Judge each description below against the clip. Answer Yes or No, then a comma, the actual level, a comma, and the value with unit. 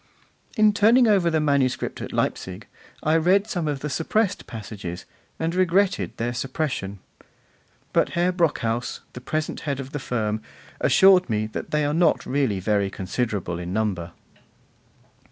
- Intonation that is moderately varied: No, wide, 8.1 semitones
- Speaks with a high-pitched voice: No, medium, 140 Hz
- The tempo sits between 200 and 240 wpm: No, average, 150 wpm